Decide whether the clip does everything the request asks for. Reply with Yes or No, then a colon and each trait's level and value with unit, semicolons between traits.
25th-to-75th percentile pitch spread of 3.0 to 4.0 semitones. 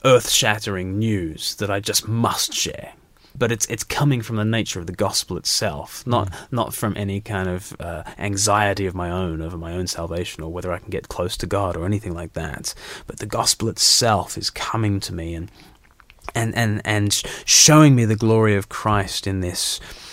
Yes: average, 3.7 semitones